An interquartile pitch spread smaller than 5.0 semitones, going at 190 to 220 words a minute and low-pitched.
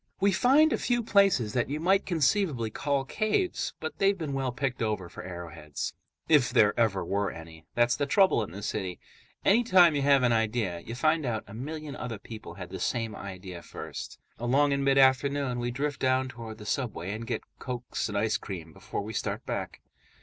No: wide, 5.6 semitones; average, 200 wpm; low, 125 Hz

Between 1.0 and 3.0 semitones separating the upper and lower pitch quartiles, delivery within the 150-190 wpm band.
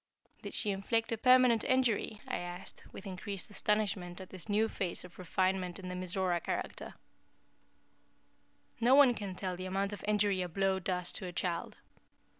Yes: narrow, 2.6 semitones; average, 170 wpm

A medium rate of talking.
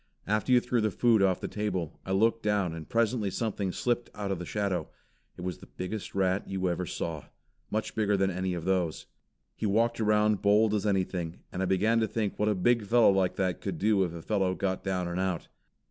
No: fast, 225 wpm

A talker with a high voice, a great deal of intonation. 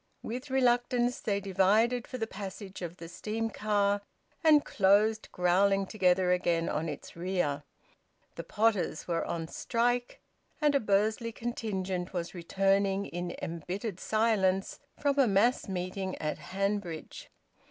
No: high, 195 Hz; average, 3.8 semitones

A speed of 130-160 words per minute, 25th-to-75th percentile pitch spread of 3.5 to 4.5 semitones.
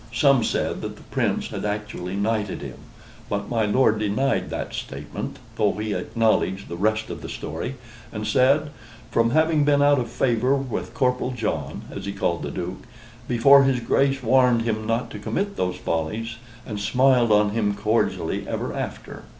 No: average, 175 wpm; average, 4.0 semitones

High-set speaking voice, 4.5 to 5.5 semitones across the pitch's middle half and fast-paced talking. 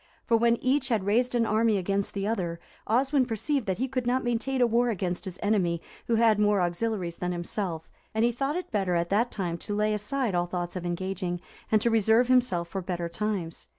Yes: high, 210 Hz; average, 4.9 semitones; fast, 220 wpm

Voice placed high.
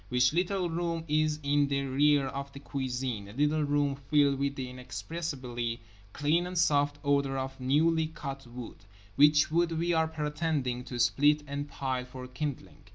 No: medium, 145 Hz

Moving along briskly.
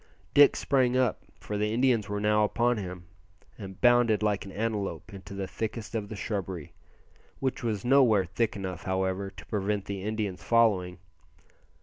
No: average, 160 wpm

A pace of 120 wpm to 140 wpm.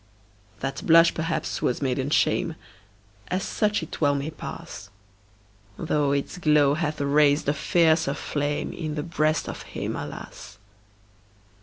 Yes: slow, 135 wpm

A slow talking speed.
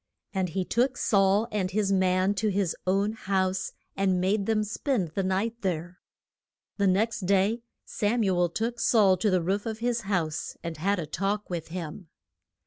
No: average, 180 wpm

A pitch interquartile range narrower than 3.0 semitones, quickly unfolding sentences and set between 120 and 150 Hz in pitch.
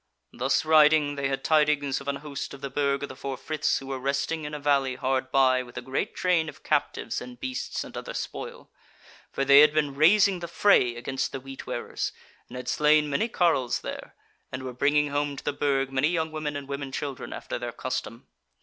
Yes: narrow, 2.4 semitones; fast, 215 wpm; medium, 140 Hz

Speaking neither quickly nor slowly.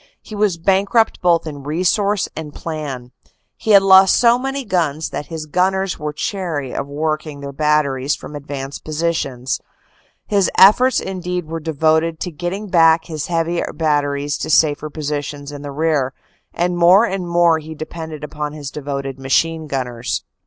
Yes: average, 160 wpm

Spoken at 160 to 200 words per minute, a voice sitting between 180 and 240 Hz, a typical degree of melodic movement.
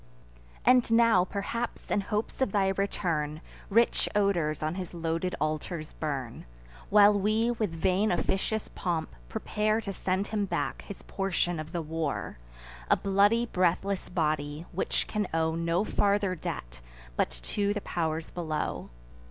No: average, 145 wpm; medium, 185 Hz; average, 4.2 semitones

